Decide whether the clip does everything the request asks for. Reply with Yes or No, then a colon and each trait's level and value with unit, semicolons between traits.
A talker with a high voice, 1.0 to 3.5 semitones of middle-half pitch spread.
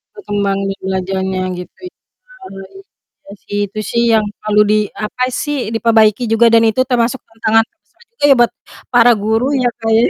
Yes: high, 225 Hz; average, 2.8 semitones